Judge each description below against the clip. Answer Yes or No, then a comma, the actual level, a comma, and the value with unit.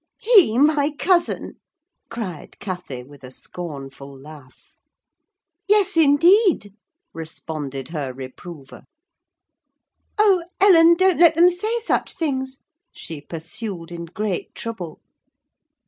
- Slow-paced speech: Yes, slow, 100 wpm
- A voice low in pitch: No, high, 210 Hz